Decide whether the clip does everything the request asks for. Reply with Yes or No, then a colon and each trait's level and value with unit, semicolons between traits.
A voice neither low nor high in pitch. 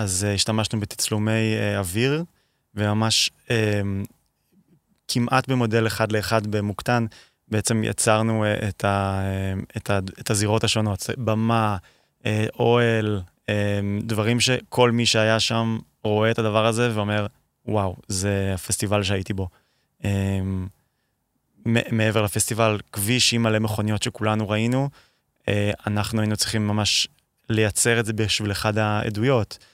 No: low, 110 Hz